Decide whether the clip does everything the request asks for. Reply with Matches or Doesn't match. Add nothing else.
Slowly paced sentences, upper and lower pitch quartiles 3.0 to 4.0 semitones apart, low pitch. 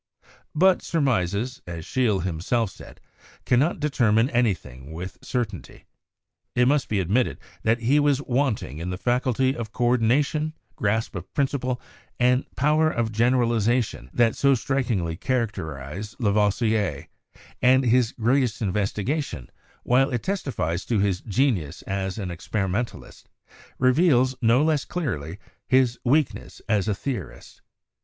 Doesn't match